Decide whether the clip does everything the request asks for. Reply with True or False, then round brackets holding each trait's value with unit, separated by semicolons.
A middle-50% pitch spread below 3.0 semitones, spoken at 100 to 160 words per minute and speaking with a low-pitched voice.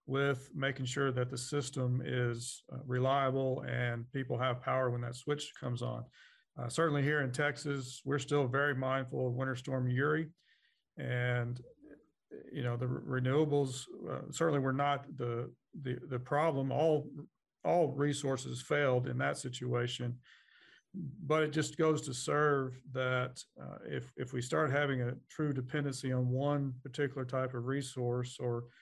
True (2.5 semitones; 155 wpm; 130 Hz)